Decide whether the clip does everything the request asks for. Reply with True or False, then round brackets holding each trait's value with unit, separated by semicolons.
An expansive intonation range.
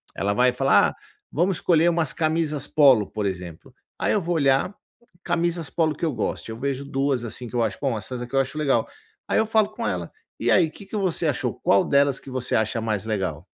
True (5.8 semitones)